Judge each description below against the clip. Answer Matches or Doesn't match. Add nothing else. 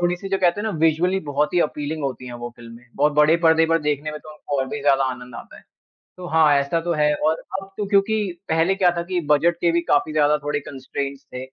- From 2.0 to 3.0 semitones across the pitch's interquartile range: Doesn't match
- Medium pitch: Matches